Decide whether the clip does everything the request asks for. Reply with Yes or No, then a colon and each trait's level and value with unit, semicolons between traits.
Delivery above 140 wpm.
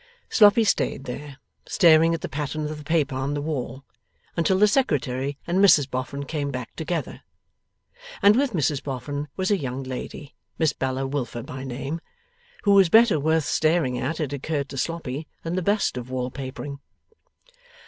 Yes: average, 170 wpm